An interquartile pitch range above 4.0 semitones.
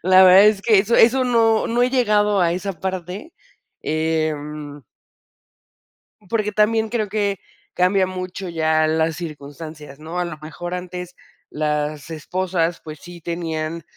Yes: average, 4.4 semitones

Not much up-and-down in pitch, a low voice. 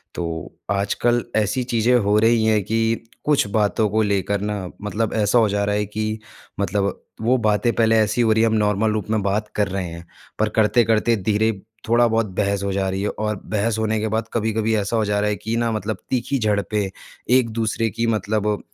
Yes: narrow, 1.6 semitones; low, 110 Hz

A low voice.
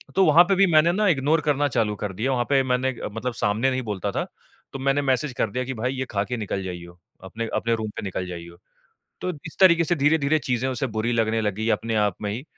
Yes: low, 125 Hz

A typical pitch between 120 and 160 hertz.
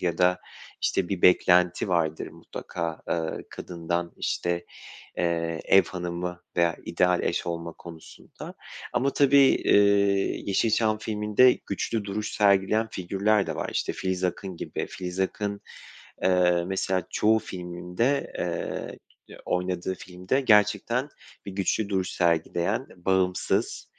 No: very low, 95 Hz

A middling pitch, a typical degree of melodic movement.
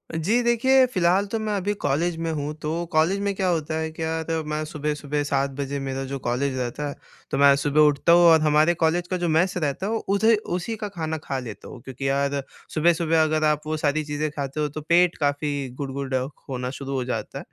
Yes: medium, 155 Hz; average, 3.5 semitones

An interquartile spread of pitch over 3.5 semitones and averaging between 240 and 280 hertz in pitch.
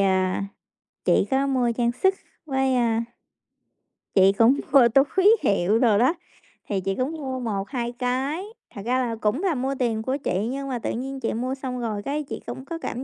No: average, 3.2 semitones; very high, 250 Hz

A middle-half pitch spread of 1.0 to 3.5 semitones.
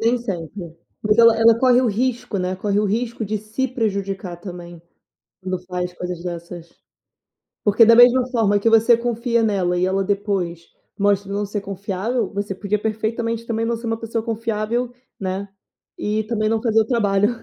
Yes: average, 3.1 semitones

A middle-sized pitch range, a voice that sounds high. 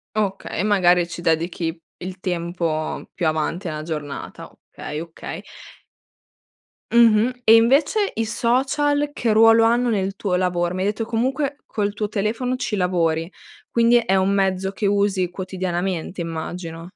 Yes: average, 4.6 semitones; high, 195 Hz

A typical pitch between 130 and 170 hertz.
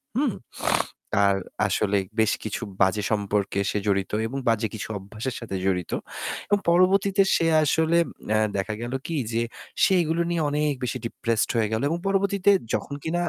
No: low, 120 Hz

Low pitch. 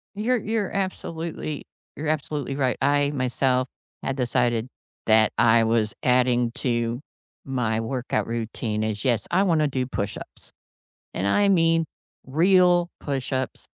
Yes: low, 130 Hz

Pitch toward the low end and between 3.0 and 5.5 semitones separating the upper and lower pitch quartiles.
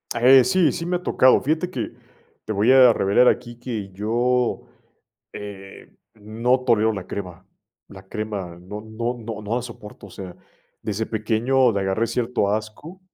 Yes: low, 110 Hz; average, 3.5 semitones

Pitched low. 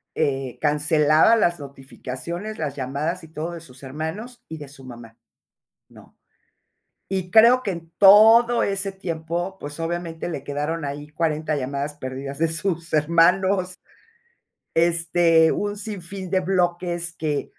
No: medium, 165 Hz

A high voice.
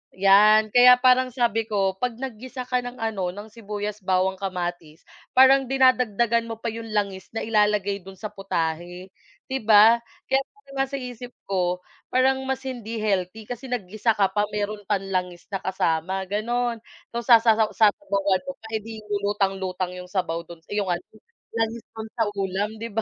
Yes: high, 210 Hz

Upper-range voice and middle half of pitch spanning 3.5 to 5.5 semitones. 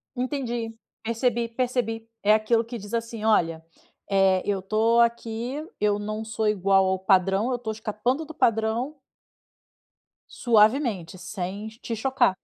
No: high, 220 Hz; average, 2.7 semitones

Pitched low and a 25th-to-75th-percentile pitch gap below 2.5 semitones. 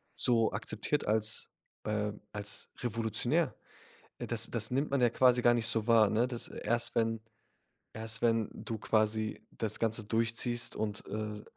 Yes: low, 115 Hz; narrow, 1.6 semitones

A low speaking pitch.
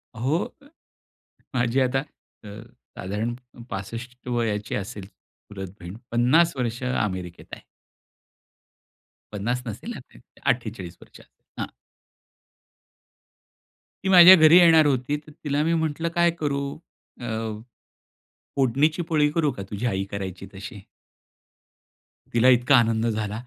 Yes: low, 120 Hz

